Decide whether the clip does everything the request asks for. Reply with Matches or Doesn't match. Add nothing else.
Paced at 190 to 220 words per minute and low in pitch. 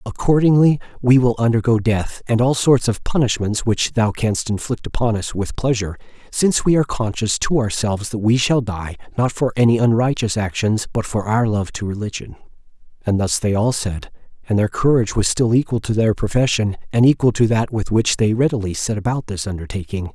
Matches